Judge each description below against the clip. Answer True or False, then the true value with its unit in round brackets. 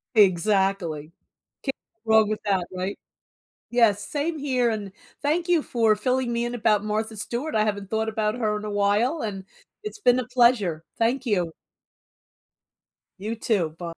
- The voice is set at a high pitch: True (215 Hz)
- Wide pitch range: False (3.4 semitones)